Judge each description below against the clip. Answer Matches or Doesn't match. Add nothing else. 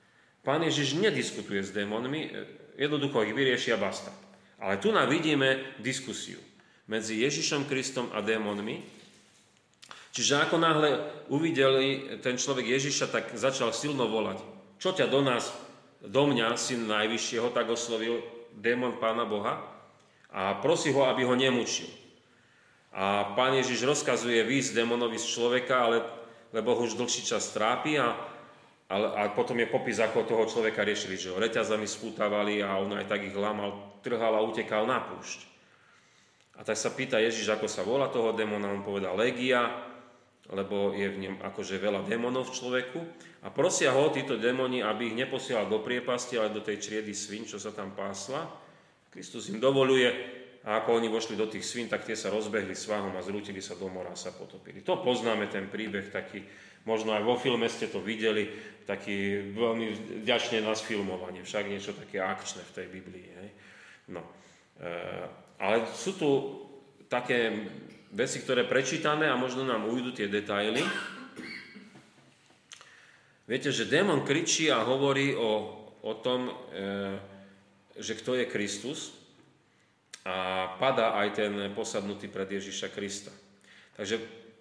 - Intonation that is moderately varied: Matches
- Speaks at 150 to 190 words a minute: Matches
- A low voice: Matches